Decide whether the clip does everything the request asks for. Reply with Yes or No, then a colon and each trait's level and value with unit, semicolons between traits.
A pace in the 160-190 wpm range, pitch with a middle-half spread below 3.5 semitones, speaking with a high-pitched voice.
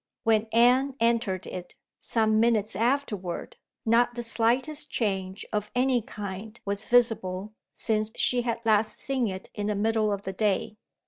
No: average, 150 wpm; average, 2.7 semitones; high, 220 Hz